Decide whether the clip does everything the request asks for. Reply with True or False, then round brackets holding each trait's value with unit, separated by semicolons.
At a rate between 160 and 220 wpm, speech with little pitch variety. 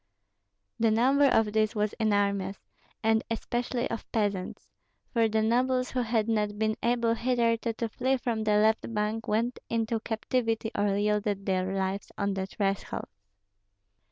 False (150 wpm; 2.0 semitones)